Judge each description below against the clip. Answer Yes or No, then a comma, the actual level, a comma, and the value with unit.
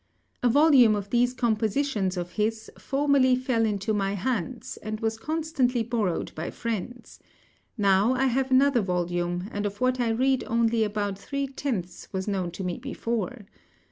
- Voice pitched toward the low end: No, high, 225 Hz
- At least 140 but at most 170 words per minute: Yes, average, 160 wpm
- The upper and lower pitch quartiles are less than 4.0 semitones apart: No, average, 4.3 semitones